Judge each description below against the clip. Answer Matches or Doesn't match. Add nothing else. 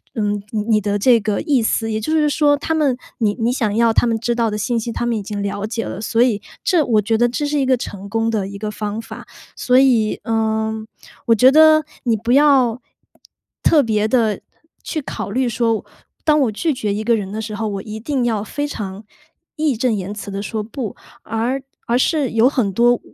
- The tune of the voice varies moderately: Matches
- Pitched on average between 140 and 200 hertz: Doesn't match